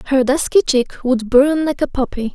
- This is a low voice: No, very high, 265 Hz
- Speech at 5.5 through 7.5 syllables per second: No, 4.9 syllables/s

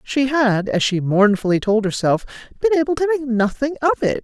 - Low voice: No, high, 240 Hz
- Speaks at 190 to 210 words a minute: Yes, average, 200 wpm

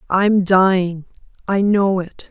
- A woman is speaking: Yes, female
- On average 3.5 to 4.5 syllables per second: Yes, 3.6 syllables/s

